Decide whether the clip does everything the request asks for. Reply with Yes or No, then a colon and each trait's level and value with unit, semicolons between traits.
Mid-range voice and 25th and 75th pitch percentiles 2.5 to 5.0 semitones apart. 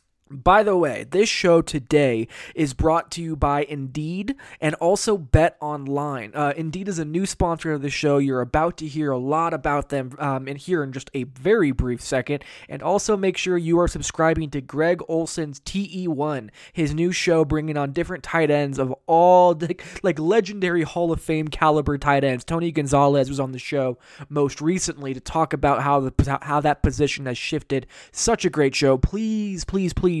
Yes: medium, 155 Hz; average, 3.4 semitones